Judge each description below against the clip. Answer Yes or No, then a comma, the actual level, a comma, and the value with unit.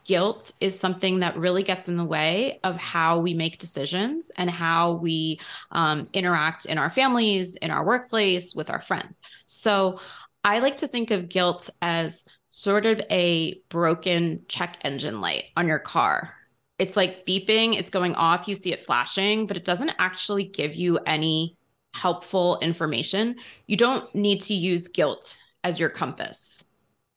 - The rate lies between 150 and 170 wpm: Yes, average, 165 wpm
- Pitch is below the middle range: No, medium, 185 Hz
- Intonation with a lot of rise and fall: No, average, 3.2 semitones